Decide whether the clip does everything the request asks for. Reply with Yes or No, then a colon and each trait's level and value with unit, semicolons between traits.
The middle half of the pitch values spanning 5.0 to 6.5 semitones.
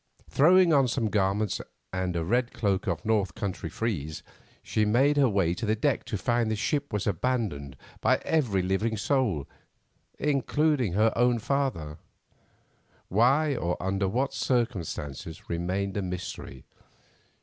Yes: wide, 5.4 semitones